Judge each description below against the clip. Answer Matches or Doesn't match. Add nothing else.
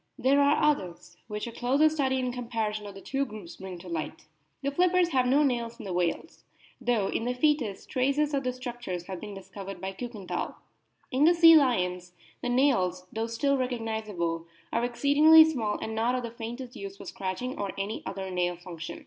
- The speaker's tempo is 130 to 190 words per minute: Doesn't match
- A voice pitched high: Matches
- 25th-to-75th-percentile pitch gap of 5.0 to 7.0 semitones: Matches